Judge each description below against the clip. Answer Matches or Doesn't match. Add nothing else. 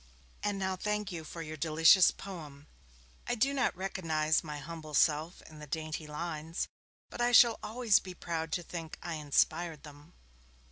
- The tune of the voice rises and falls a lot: Doesn't match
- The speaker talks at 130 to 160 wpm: Doesn't match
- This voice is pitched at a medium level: Matches